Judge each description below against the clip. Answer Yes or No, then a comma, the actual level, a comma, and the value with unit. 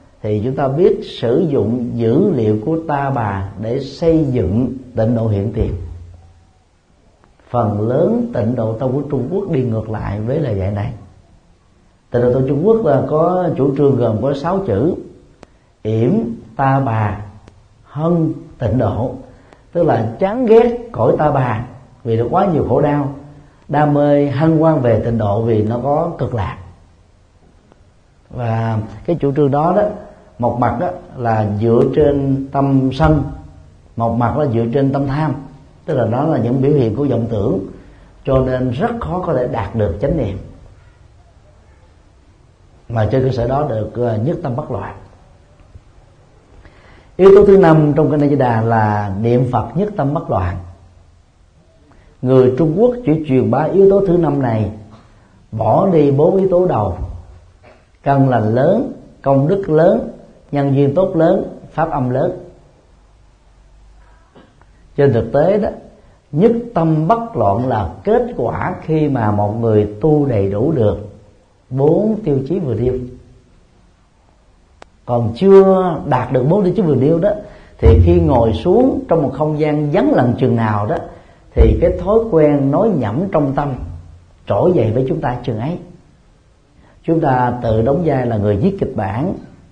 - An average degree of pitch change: No, wide, 6.2 semitones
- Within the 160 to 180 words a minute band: Yes, slow, 165 wpm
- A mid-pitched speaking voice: No, low, 125 Hz